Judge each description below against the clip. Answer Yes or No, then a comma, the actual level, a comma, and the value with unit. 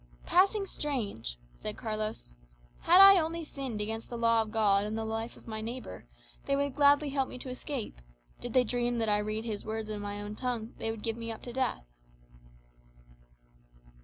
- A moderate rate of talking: Yes, average, 190 wpm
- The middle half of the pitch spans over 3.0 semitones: Yes, average, 3.7 semitones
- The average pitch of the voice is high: Yes, high, 230 Hz